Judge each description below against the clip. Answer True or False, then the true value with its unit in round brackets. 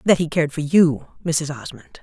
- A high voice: False (155 Hz)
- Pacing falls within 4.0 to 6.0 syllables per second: True (5.2 syllables/s)